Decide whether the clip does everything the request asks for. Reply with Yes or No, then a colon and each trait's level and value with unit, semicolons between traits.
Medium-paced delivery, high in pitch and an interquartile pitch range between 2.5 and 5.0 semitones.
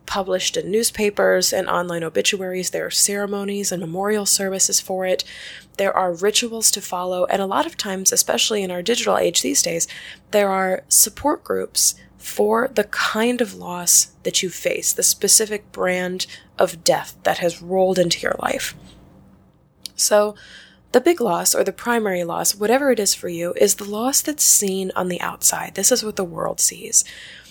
Yes: average, 175 wpm; high, 200 Hz; average, 3.1 semitones